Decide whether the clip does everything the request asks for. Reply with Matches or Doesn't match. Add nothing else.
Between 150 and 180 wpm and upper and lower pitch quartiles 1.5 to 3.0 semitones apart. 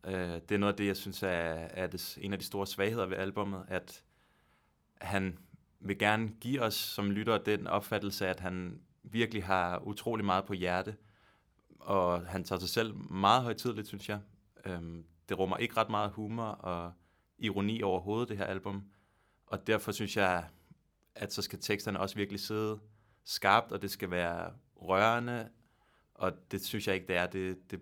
Matches